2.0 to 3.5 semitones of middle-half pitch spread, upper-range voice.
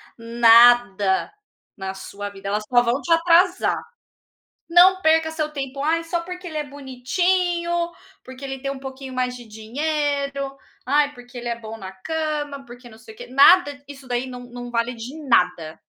No: average, 4.6 semitones; very high, 265 Hz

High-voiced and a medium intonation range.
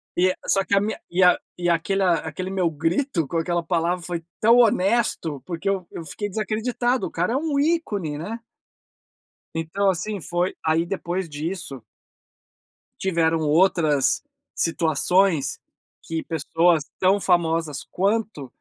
No: medium, 175 Hz; average, 3.4 semitones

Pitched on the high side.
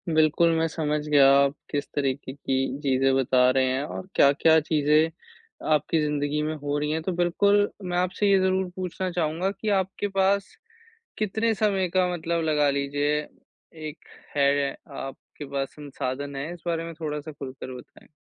No: medium, 155 Hz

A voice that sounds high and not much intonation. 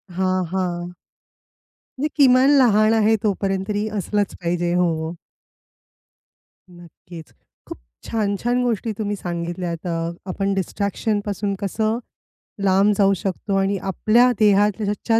No: high, 200 Hz; average, 3.2 semitones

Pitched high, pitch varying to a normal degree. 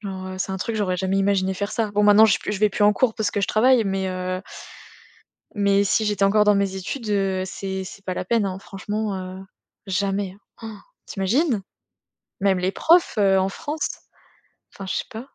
No: high, 200 Hz; narrow, 1.9 semitones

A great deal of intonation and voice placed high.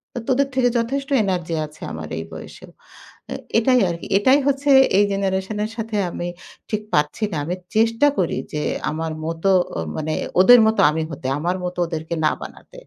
Yes: wide, 6.1 semitones; high, 195 Hz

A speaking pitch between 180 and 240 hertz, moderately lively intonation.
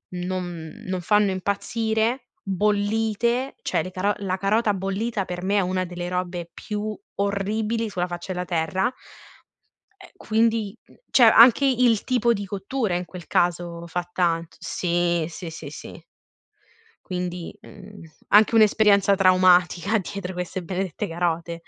Yes: high, 190 Hz; average, 3.3 semitones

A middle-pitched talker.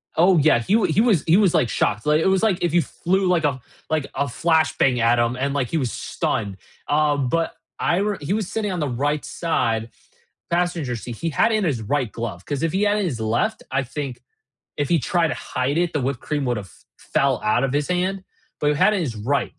Yes: medium, 150 Hz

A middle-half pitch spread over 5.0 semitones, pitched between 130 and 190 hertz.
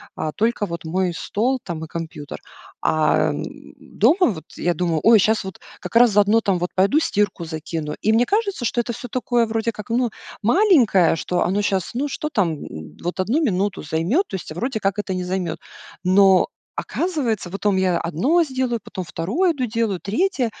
No: wide, 5.4 semitones; high, 205 Hz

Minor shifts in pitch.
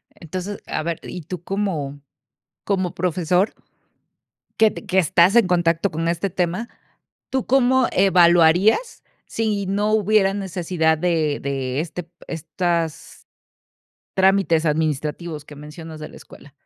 No: average, 3.5 semitones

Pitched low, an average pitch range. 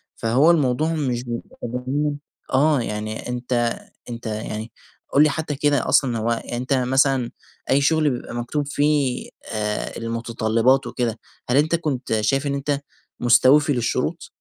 Yes: low, 130 Hz; average, 3.6 semitones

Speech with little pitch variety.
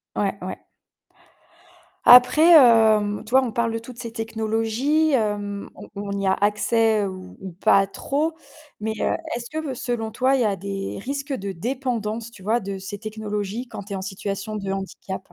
No: average, 3.3 semitones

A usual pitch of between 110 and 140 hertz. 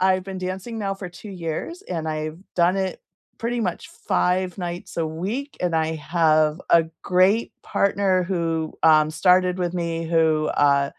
No: medium, 175 Hz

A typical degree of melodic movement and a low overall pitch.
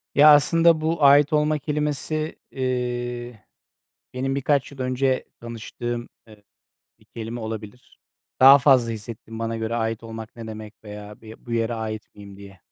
Yes: average, 3.8 semitones; low, 120 Hz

